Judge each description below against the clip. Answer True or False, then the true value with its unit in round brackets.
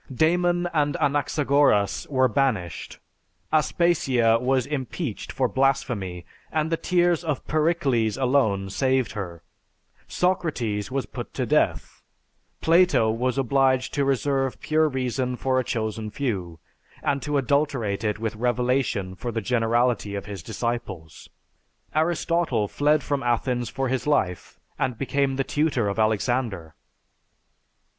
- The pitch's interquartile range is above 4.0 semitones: True (4.5 semitones)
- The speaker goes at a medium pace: False (125 wpm)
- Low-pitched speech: True (130 Hz)